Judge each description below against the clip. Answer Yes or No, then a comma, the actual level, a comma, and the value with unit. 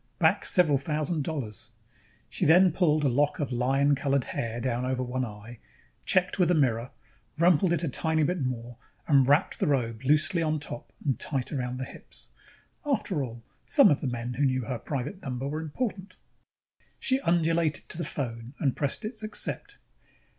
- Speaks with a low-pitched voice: No, medium, 145 Hz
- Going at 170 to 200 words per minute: Yes, average, 180 wpm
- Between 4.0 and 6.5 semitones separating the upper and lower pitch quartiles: Yes, average, 4.6 semitones